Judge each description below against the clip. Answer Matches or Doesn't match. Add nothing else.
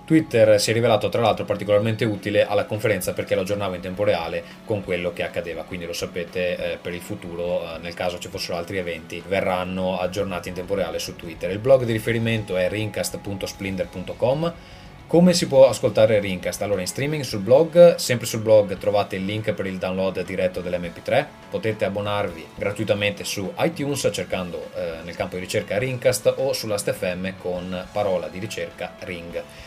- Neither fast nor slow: Doesn't match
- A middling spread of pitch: Doesn't match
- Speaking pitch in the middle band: Doesn't match